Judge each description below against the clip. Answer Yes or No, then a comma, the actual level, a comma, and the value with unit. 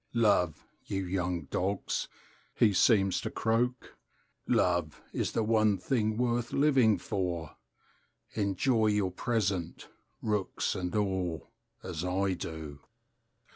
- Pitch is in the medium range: No, very low, 95 Hz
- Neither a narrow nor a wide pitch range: Yes, average, 3.7 semitones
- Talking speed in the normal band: No, slow, 110 wpm